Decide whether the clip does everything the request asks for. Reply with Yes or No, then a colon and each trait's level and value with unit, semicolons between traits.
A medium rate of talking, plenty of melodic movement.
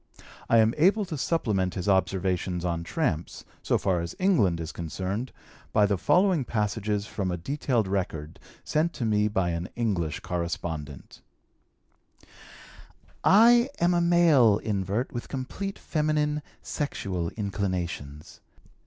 No: slow, 125 wpm; wide, 8.9 semitones